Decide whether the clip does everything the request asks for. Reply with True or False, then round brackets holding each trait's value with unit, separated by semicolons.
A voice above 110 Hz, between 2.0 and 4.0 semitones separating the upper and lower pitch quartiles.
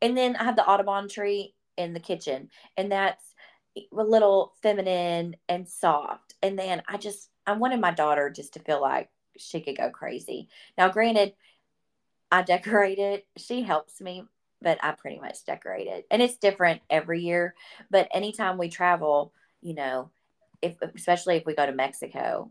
True (185 Hz; 3.1 semitones)